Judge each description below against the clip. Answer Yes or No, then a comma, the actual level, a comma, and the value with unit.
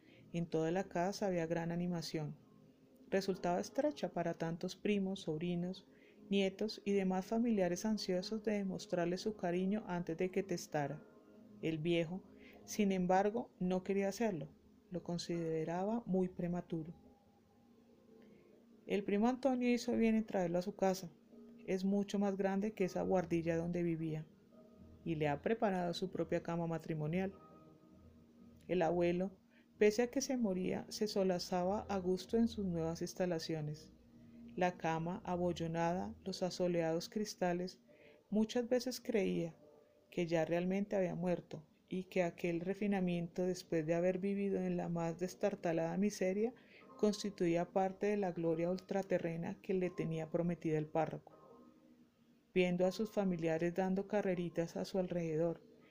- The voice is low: No, medium, 185 Hz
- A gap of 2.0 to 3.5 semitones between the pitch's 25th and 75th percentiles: Yes, average, 3.2 semitones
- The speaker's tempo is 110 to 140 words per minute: Yes, average, 135 wpm